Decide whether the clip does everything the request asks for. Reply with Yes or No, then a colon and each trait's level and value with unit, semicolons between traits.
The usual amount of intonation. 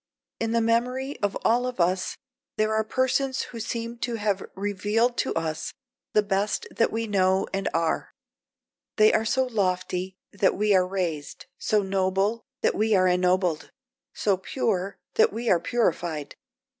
Yes: average, 3.6 semitones